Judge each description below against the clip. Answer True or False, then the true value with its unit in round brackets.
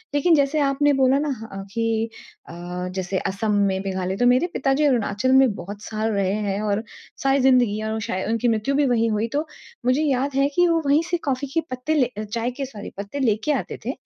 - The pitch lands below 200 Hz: False (245 Hz)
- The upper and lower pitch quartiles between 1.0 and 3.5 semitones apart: False (4.7 semitones)